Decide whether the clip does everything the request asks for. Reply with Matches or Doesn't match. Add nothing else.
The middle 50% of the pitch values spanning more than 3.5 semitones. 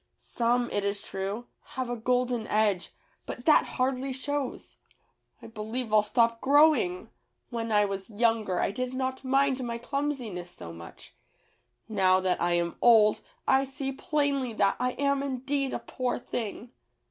Matches